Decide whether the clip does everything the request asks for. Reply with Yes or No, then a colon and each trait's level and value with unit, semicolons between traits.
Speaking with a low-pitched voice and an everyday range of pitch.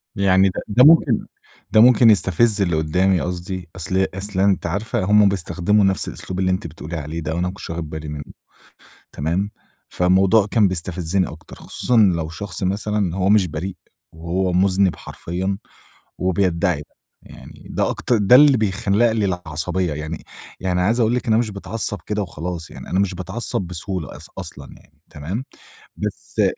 Yes: very low, 95 Hz; average, 3.1 semitones